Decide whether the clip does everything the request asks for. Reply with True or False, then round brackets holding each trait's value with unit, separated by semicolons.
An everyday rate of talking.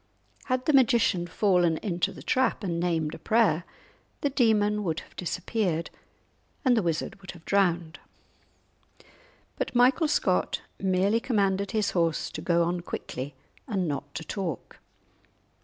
True (145 wpm)